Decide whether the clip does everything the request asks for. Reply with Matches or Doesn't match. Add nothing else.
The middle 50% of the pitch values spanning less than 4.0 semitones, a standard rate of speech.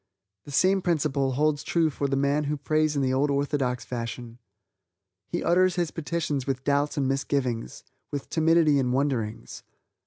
Matches